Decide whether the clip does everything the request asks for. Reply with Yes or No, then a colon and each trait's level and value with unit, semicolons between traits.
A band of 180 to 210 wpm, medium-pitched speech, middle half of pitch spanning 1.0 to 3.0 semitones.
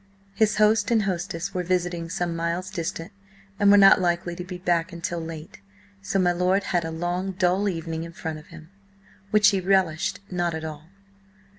Yes: average, 185 wpm; medium, 175 Hz; narrow, 2.4 semitones